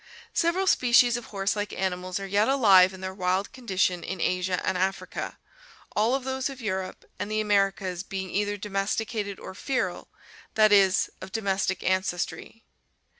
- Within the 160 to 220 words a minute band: Yes, average, 165 wpm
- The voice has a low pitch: No, high, 195 Hz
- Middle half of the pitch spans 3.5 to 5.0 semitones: No, average, 2.7 semitones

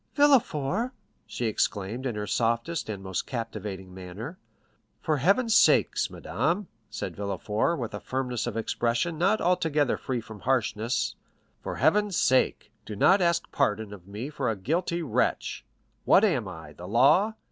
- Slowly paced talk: No, average, 145 wpm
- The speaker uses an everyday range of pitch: No, wide, 8.2 semitones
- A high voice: No, low, 125 Hz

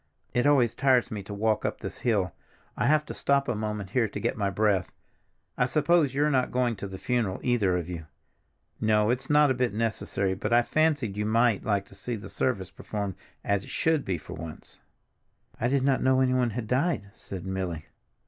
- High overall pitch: No, low, 115 Hz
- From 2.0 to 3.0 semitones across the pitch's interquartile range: No, average, 4.6 semitones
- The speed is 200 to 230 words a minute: Yes, fast, 205 wpm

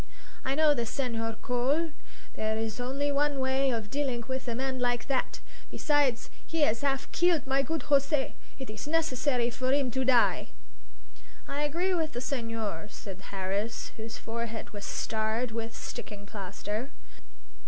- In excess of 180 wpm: No, average, 155 wpm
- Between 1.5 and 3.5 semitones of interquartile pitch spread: No, average, 3.9 semitones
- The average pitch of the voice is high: Yes, very high, 255 Hz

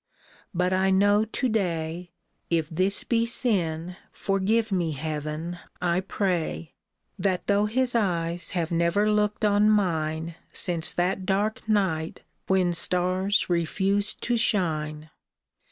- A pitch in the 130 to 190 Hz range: Yes, medium, 185 Hz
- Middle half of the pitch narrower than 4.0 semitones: Yes, average, 3.6 semitones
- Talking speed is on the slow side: Yes, slow, 130 wpm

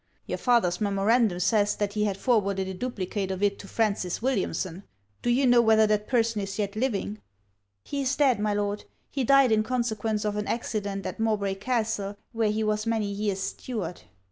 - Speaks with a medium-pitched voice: No, high, 210 Hz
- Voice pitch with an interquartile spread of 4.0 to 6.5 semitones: No, narrow, 2.5 semitones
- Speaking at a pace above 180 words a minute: Yes, average, 190 wpm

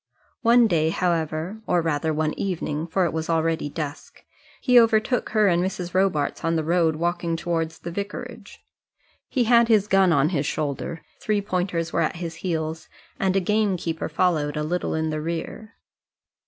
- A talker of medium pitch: Yes, medium, 170 Hz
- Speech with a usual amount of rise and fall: Yes, average, 3.5 semitones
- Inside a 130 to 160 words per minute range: No, average, 170 wpm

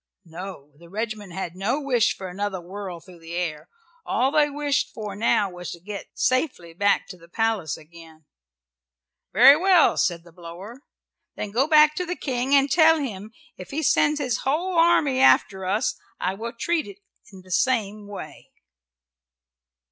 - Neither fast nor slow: Yes, average, 170 wpm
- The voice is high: Yes, high, 210 Hz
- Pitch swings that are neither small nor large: No, wide, 7.3 semitones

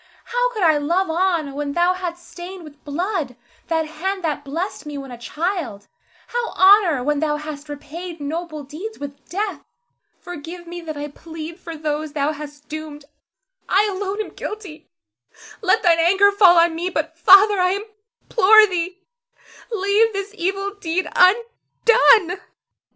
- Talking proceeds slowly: No, average, 155 wpm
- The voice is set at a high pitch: Yes, very high, 345 Hz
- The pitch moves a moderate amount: Yes, average, 4.3 semitones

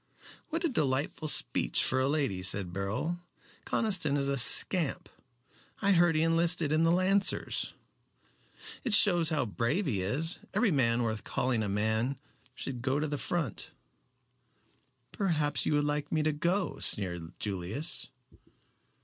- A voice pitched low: No, medium, 145 Hz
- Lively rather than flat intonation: Yes, wide, 6.4 semitones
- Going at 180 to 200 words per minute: No, average, 145 wpm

